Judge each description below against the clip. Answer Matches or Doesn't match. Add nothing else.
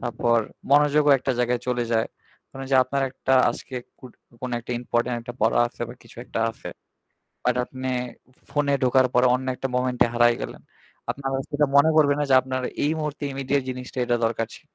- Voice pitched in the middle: Doesn't match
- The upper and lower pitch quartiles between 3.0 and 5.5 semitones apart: Doesn't match